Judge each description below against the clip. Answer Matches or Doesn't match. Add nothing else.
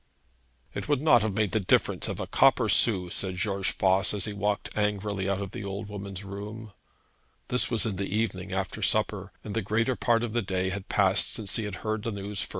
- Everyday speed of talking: Doesn't match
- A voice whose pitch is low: Matches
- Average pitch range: Doesn't match